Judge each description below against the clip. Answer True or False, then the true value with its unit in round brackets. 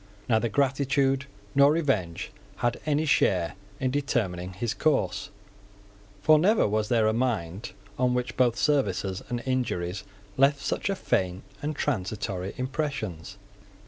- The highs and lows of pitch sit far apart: True (6.4 semitones)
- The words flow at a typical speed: False (125 wpm)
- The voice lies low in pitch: True (120 Hz)